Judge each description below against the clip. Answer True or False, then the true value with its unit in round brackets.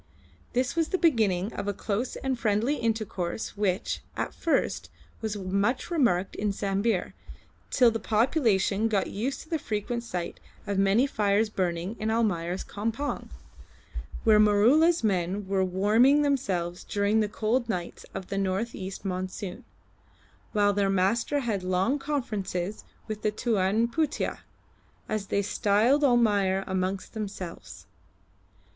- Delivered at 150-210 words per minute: False (135 wpm)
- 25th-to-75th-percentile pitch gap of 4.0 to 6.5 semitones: False (3.4 semitones)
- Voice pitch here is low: False (210 Hz)